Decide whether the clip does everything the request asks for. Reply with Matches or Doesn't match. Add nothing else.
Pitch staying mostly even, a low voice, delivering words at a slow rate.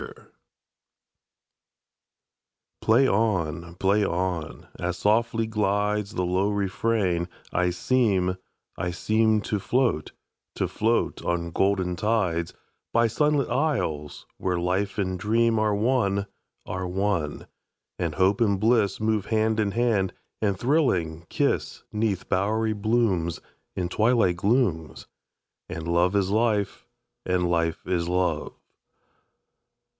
Doesn't match